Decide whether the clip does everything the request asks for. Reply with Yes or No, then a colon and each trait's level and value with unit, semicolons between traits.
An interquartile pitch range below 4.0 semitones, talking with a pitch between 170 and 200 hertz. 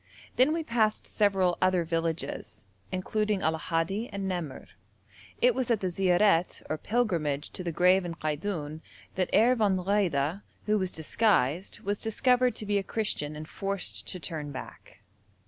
No: average, 4.4 semitones; medium, 185 Hz